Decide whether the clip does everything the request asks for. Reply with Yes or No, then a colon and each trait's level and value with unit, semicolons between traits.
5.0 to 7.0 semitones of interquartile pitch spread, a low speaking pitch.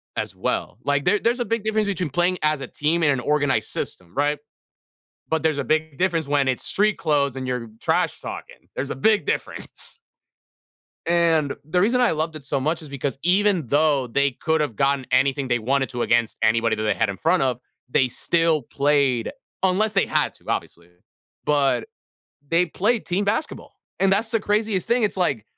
No: wide, 5.4 semitones; medium, 150 Hz